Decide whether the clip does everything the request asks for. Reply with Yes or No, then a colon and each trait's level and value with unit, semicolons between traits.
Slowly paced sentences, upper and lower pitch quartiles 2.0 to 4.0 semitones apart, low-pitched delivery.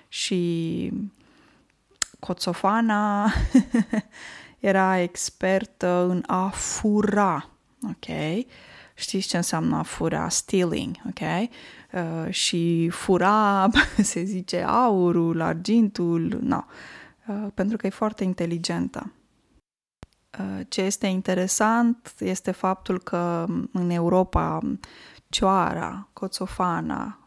No: slow, 90 wpm; average, 3.2 semitones; high, 190 Hz